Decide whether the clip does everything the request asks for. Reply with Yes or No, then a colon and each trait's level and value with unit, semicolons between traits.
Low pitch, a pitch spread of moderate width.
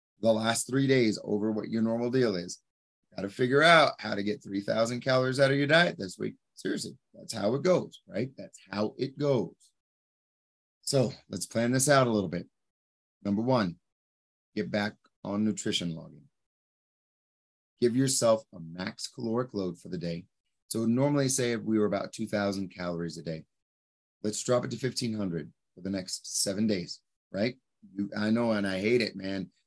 Yes: low, 105 Hz; average, 4.3 semitones